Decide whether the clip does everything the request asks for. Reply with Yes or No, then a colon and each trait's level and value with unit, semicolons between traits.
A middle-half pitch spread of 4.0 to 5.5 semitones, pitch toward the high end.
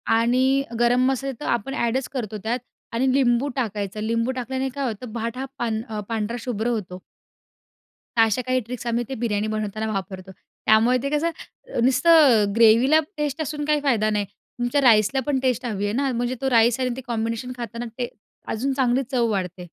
No: average, 3.2 semitones; high, 240 Hz